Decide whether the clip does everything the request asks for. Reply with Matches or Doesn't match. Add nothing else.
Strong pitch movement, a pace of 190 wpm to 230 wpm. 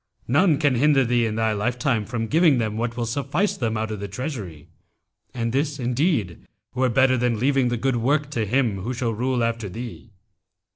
Doesn't match